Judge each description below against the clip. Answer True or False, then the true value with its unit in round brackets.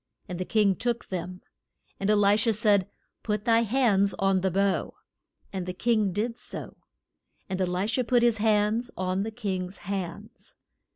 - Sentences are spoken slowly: False (175 wpm)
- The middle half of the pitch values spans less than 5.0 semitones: True (3.0 semitones)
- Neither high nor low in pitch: False (205 Hz)